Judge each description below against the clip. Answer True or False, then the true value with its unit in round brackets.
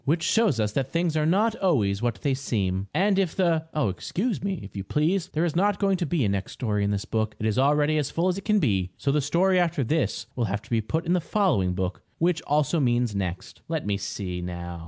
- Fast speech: True (255 wpm)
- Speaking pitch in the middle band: True (145 Hz)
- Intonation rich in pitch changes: True (9.0 semitones)